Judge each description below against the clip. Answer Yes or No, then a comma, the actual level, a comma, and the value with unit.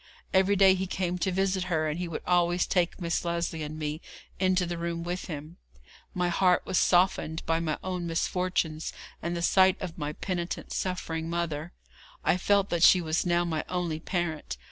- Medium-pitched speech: Yes, medium, 175 Hz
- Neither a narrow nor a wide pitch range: No, narrow, 2.0 semitones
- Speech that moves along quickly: No, average, 190 wpm